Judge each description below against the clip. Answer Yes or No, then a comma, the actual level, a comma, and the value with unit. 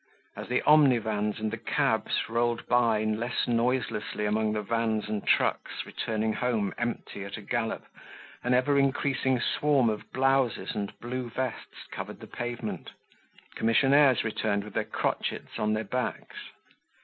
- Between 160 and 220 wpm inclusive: No, average, 145 wpm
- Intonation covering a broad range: No, average, 2.8 semitones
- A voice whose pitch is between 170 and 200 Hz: No, low, 115 Hz